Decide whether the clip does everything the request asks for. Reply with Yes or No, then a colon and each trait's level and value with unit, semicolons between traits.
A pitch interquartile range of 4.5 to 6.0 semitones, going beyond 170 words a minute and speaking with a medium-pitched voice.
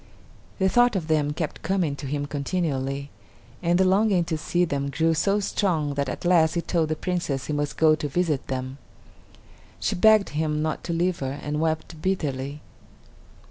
No: average, 3.7 semitones; average, 180 wpm; medium, 155 Hz